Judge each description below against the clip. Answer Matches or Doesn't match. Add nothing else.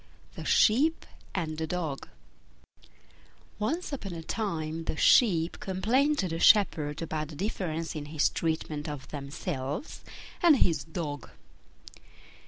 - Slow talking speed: Matches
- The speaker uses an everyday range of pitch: Matches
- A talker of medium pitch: Matches